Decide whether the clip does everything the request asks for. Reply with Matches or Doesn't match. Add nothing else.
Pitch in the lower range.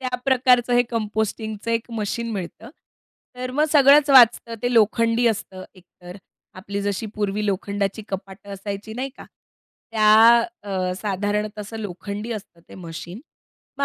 Doesn't match